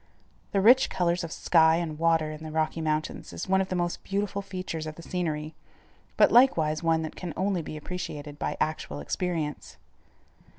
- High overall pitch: No, medium, 165 Hz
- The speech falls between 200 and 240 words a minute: No, average, 180 wpm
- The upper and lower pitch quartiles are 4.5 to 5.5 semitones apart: No, average, 2.9 semitones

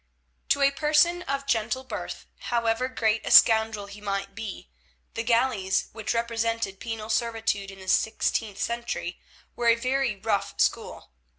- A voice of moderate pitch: No, high, 225 Hz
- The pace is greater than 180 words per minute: No, average, 150 wpm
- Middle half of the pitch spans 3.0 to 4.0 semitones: No, narrow, 2.5 semitones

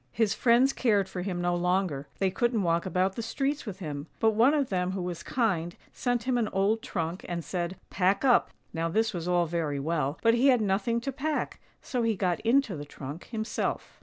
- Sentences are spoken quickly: Yes, fast, 220 wpm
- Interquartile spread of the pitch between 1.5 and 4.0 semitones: No, average, 5.0 semitones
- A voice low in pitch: No, high, 195 Hz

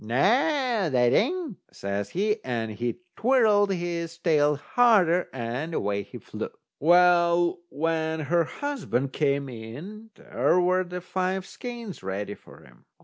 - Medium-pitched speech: Yes, medium, 170 Hz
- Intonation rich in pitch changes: Yes, wide, 7.3 semitones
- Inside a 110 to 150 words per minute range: Yes, slow, 135 wpm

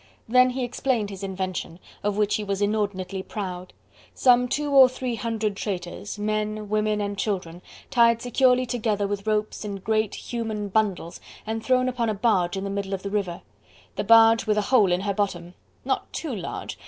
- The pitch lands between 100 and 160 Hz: No, high, 210 Hz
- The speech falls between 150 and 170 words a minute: No, average, 185 wpm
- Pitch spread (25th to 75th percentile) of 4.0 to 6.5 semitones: No, average, 2.8 semitones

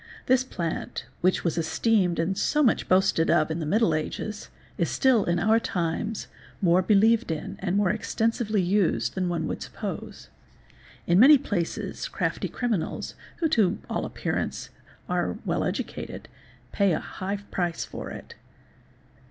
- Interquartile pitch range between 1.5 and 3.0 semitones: No, average, 4.5 semitones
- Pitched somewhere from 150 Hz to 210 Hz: Yes, high, 190 Hz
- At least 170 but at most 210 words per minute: No, average, 150 wpm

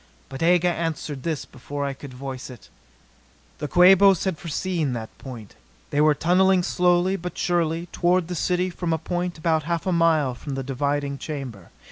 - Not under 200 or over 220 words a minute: No, average, 175 wpm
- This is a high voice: No, medium, 160 Hz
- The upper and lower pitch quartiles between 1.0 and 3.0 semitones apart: No, average, 4.1 semitones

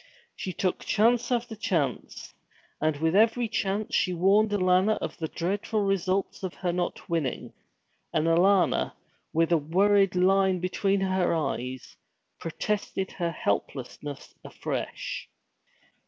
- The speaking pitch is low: No, medium, 185 Hz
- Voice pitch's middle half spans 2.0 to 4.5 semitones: Yes, average, 3.4 semitones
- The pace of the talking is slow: Yes, slow, 125 wpm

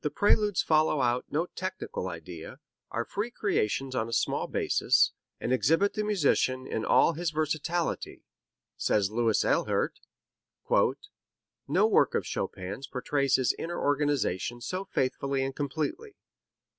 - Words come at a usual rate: No, slow, 130 wpm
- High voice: No, medium, 140 Hz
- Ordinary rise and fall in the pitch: No, wide, 6.0 semitones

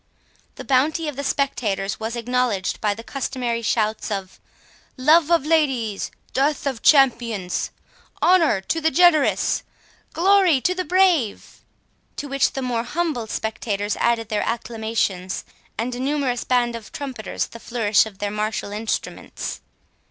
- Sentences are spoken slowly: Yes, slow, 130 wpm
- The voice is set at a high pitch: Yes, high, 245 Hz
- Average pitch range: Yes, average, 4.9 semitones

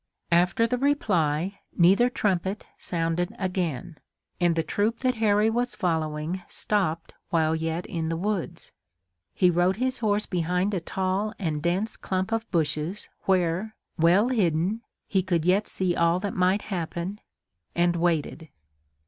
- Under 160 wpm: Yes, average, 140 wpm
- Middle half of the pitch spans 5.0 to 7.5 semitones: No, average, 3.7 semitones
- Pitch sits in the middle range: Yes, medium, 180 Hz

